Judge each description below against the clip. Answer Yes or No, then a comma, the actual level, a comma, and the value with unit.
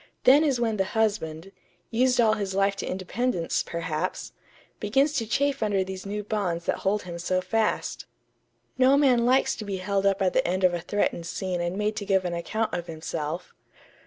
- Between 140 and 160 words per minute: No, average, 195 wpm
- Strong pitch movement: No, average, 3.8 semitones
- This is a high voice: Yes, high, 195 Hz